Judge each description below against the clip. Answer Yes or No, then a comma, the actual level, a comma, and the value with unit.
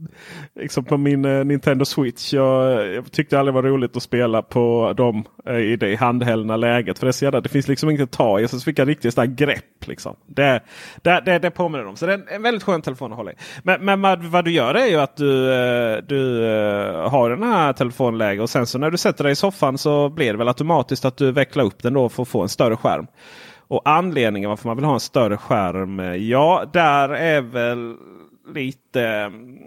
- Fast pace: Yes, fast, 220 wpm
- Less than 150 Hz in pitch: Yes, low, 135 Hz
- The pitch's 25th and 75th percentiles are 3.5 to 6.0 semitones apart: Yes, average, 3.8 semitones